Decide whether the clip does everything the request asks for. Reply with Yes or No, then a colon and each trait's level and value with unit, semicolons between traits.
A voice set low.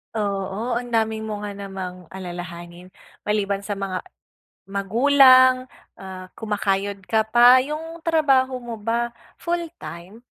No: high, 210 Hz